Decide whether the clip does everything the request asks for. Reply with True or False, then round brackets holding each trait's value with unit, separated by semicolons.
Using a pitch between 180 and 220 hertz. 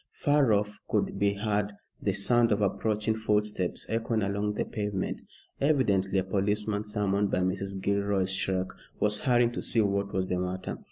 False (105 Hz)